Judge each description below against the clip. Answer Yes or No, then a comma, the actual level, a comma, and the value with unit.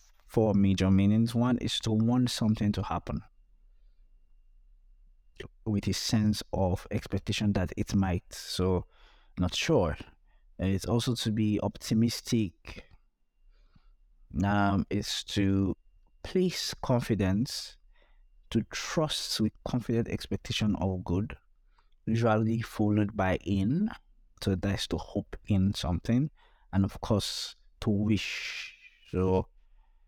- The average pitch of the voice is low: Yes, low, 100 Hz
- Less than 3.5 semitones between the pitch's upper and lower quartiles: Yes, average, 3.1 semitones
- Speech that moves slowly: Yes, slow, 110 wpm